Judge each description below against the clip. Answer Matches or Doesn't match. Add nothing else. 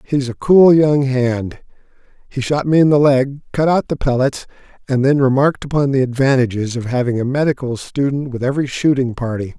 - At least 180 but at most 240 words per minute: Matches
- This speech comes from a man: Matches